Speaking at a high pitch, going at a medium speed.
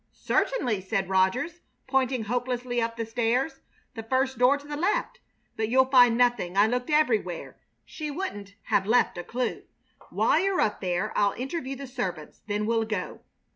Yes: high, 245 Hz; average, 170 wpm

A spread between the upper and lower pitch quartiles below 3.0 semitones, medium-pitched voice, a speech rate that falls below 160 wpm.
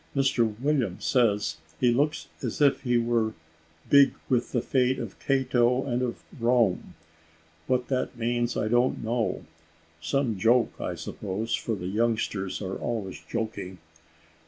No: narrow, 2.6 semitones; low, 120 Hz; average, 140 wpm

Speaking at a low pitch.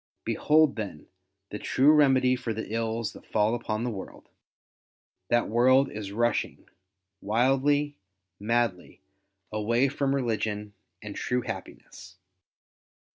Yes: low, 120 Hz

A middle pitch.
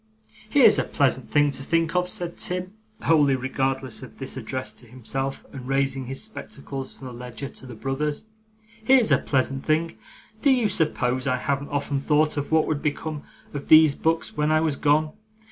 Yes: medium, 145 Hz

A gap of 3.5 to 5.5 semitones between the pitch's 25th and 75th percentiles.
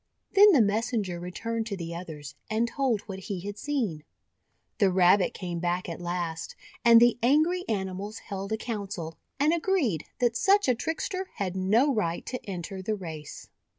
Yes: average, 5.2 semitones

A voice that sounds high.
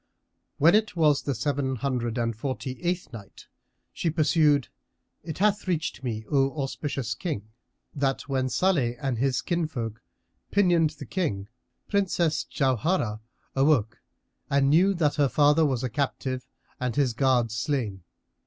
No: medium, 140 Hz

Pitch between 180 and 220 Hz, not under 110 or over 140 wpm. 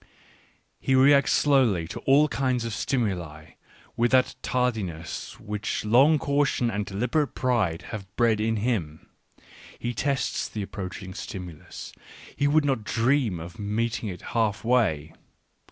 No: low, 115 Hz; slow, 135 wpm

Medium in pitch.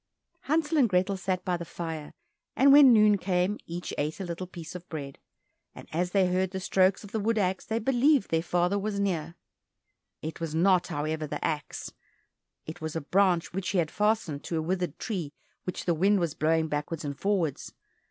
Yes: medium, 180 Hz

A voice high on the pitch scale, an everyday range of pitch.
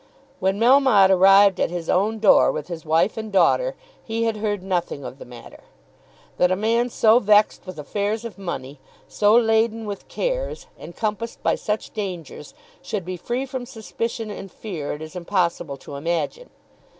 Yes: high, 205 Hz; average, 4.3 semitones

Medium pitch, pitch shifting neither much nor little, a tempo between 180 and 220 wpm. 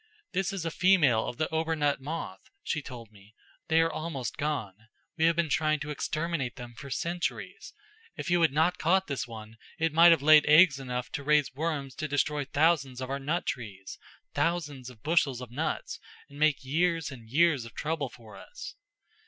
Yes: medium, 150 Hz; average, 4.3 semitones; average, 195 wpm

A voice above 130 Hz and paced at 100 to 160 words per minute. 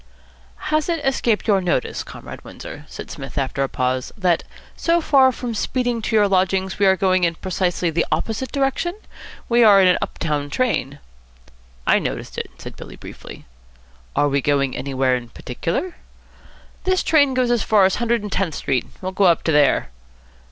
No: high, 190 Hz; average, 180 wpm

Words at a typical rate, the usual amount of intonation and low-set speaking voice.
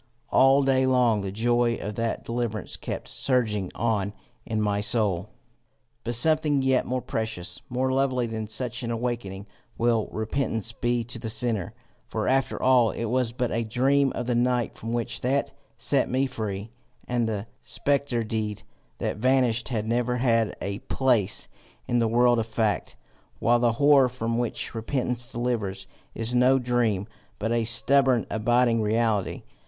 No: average, 160 wpm; narrow, 2.3 semitones; low, 120 Hz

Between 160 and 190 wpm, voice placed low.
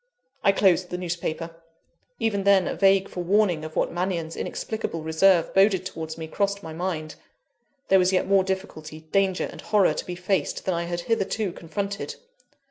No: average, 170 wpm; medium, 185 Hz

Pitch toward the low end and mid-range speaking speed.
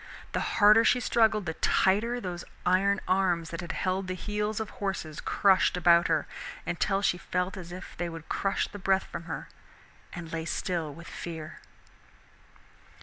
No: medium, 185 Hz; average, 165 wpm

